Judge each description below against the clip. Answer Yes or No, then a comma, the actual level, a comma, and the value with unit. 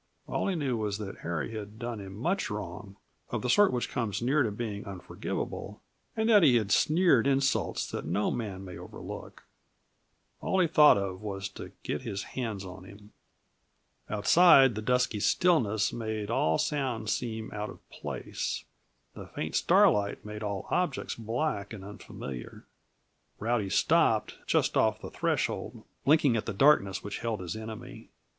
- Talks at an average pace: Yes, average, 160 wpm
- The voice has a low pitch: Yes, low, 110 Hz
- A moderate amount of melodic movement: Yes, average, 4.3 semitones